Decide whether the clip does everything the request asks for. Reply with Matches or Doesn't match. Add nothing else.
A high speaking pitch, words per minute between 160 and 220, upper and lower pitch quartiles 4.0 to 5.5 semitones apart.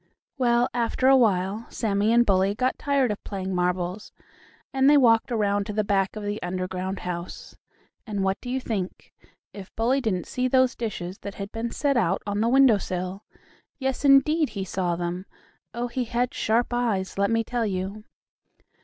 Matches